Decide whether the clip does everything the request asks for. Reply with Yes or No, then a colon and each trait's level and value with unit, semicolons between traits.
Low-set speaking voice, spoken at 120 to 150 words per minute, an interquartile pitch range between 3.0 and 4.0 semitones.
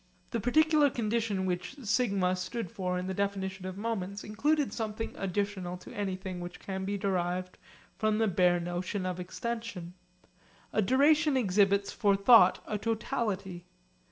No: high, 200 Hz; average, 145 wpm; average, 3.6 semitones